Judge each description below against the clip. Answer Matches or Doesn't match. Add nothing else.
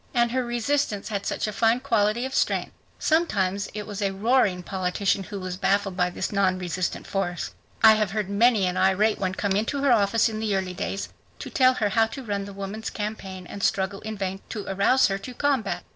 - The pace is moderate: Doesn't match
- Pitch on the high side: Matches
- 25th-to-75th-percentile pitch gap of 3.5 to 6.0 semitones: Doesn't match